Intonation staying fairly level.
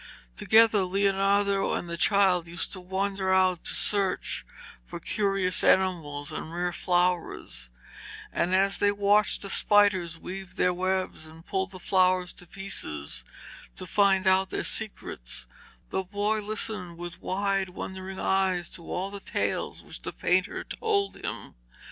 Yes: narrow, 2.0 semitones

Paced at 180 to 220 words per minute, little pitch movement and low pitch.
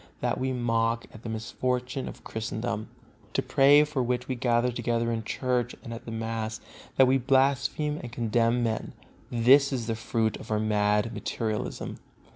No: average, 170 wpm; narrow, 2.2 semitones; low, 120 Hz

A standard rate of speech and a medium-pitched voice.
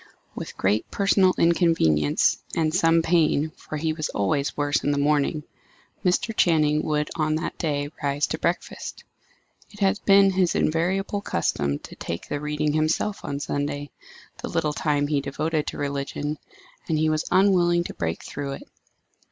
Yes: average, 160 wpm; medium, 155 Hz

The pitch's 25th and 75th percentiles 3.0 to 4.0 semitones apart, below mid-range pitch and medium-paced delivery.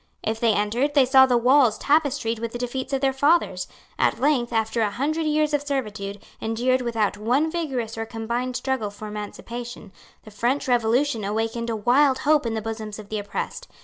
No: average, 3.6 semitones; high, 240 Hz; average, 190 wpm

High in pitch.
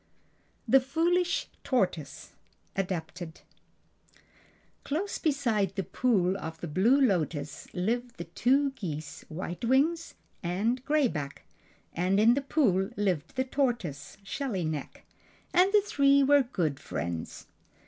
Yes: high, 215 Hz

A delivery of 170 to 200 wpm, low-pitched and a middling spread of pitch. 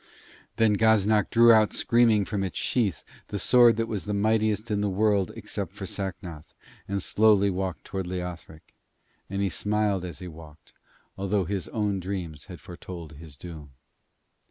No: average, 160 wpm; low, 100 Hz; average, 3.2 semitones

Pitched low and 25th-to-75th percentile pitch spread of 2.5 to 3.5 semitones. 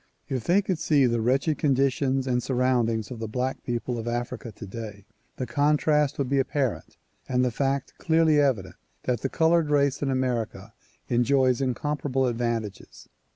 Yes: low, 130 Hz; average, 3.1 semitones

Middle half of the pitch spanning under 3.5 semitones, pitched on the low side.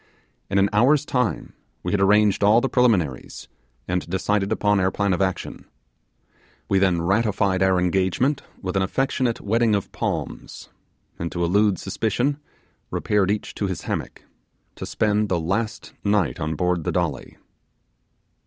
Yes: narrow, 2.6 semitones; low, 100 Hz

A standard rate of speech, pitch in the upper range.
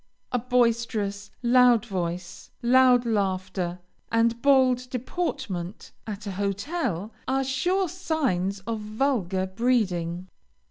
No: slow, 100 wpm; high, 230 Hz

